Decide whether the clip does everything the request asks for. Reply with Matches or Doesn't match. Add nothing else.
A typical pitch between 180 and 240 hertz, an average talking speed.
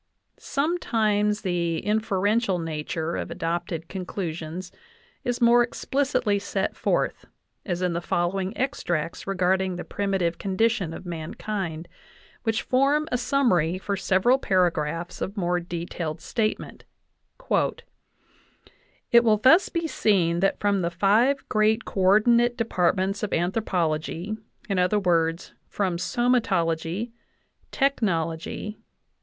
Doesn't match